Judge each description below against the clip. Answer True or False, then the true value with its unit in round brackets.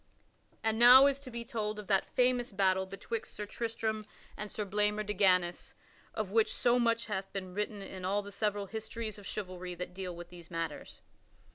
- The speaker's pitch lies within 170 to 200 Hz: False (210 Hz)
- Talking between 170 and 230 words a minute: True (190 wpm)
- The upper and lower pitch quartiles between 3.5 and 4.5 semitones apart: False (2.9 semitones)